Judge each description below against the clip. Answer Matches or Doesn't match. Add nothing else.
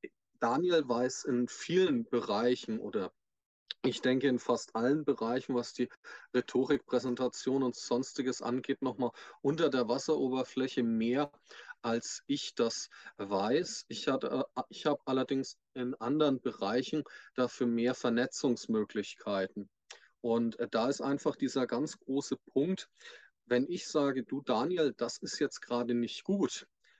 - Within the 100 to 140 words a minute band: Matches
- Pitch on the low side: Matches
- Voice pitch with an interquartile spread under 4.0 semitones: Matches